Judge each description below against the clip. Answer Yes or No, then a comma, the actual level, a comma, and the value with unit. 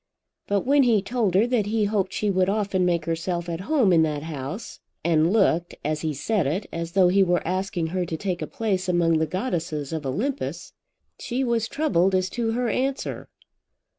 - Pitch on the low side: No, medium, 185 Hz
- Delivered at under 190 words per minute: No, average, 195 wpm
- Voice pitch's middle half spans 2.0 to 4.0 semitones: No, average, 4.8 semitones